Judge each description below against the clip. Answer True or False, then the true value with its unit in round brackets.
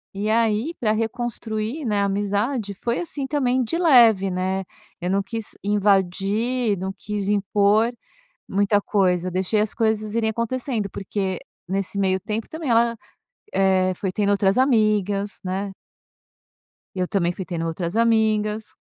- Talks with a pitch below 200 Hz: False (210 Hz)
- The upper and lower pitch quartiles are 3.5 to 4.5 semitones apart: False (2.8 semitones)